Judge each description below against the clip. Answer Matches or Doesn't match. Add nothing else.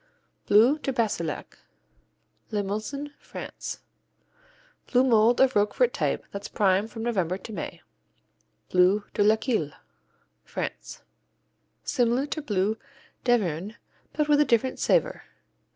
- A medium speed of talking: Doesn't match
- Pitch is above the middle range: Matches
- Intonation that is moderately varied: Matches